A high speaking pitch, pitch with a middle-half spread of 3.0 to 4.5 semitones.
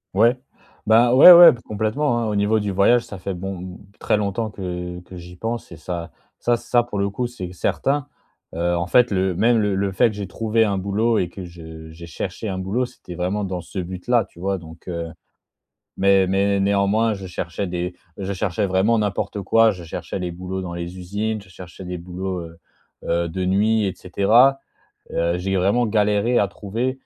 No: very low, 95 Hz; average, 3.5 semitones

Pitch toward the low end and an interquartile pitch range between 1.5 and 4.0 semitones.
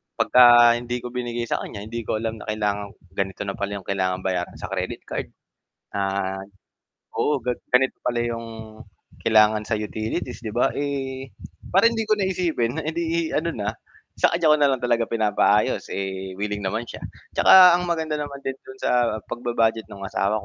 No: low, 115 Hz; average, 4.8 semitones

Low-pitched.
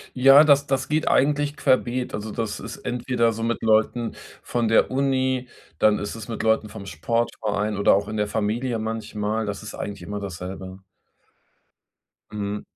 Yes: low, 110 Hz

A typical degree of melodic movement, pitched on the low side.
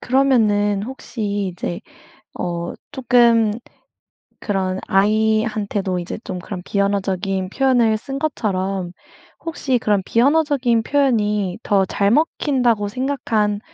No: average, 4.2 semitones; high, 210 Hz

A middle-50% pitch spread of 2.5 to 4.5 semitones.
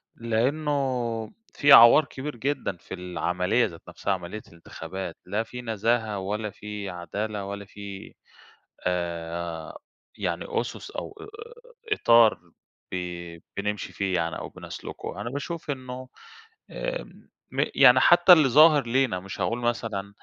No: average, 5.1 semitones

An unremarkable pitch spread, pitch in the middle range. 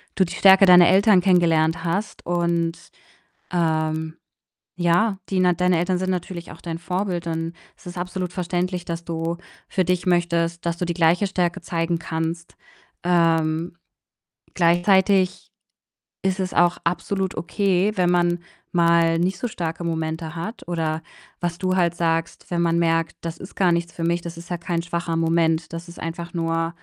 No: narrow, 1.5 semitones; medium, 170 Hz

